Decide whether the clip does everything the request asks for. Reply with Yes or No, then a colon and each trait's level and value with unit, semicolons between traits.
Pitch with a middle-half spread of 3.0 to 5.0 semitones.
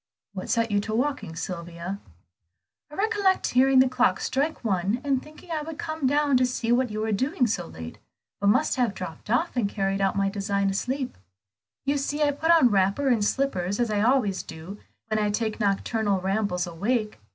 No: wide, 5.5 semitones